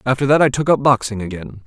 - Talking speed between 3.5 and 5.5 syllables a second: No, 6.5 syllables/s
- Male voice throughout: Yes, male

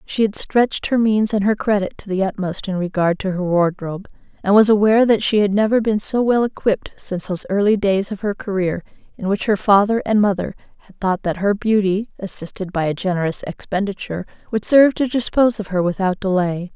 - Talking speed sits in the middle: No, fast, 210 wpm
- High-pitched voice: Yes, high, 200 Hz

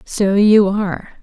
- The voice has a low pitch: No, high, 200 Hz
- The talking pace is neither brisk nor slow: Yes, average, 145 wpm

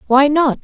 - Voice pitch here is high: Yes, very high, 280 Hz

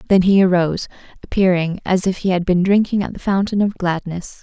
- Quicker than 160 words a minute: Yes, fast, 205 wpm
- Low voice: No, medium, 185 Hz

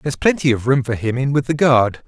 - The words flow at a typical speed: No, fast, 290 wpm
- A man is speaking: Yes, male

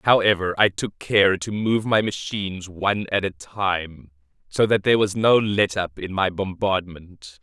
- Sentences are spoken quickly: No, average, 180 wpm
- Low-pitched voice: Yes, very low, 95 Hz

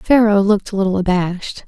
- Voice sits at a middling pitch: No, high, 200 Hz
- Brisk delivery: No, average, 180 wpm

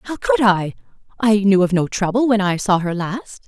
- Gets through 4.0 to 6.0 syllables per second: Yes, 4.8 syllables/s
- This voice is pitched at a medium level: No, high, 205 Hz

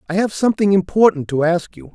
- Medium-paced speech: No, fast, 215 wpm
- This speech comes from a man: Yes, male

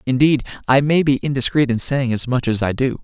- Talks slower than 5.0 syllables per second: No, 5.7 syllables/s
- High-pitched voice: No, low, 130 Hz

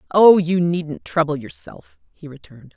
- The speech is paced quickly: No, average, 150 wpm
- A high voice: No, medium, 165 Hz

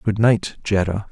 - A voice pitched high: No, low, 105 Hz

